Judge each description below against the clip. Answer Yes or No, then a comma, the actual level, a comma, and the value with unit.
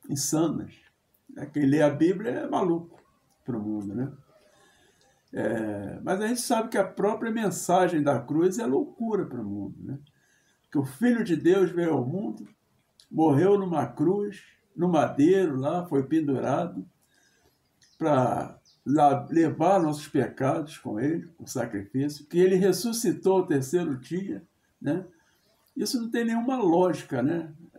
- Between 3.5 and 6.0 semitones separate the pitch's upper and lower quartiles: Yes, wide, 5.6 semitones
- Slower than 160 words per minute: Yes, average, 145 wpm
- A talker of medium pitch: Yes, medium, 170 Hz